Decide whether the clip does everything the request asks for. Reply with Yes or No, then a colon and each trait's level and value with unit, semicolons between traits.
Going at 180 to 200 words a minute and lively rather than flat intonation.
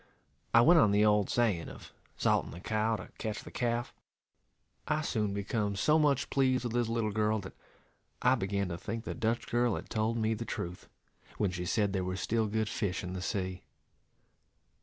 No: average, 195 wpm; average, 3.0 semitones